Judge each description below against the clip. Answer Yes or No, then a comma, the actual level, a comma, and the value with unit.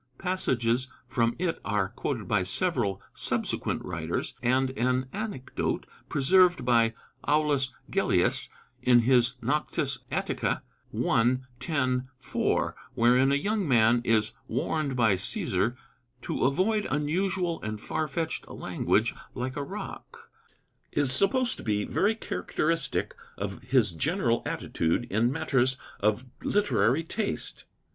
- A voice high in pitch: No, low, 130 Hz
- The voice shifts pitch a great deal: Yes, wide, 5.7 semitones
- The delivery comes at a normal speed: No, slow, 120 wpm